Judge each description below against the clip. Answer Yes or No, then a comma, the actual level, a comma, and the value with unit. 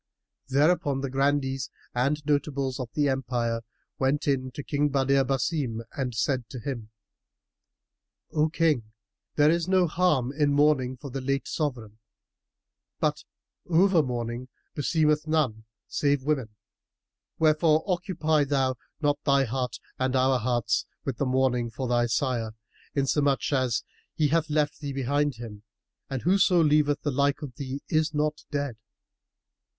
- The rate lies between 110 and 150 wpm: Yes, average, 140 wpm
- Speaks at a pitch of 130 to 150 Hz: Yes, medium, 140 Hz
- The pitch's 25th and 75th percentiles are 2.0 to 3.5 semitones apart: Yes, average, 2.8 semitones